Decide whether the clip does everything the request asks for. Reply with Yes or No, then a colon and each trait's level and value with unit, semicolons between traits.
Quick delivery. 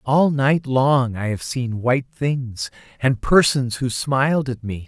No: average, 170 wpm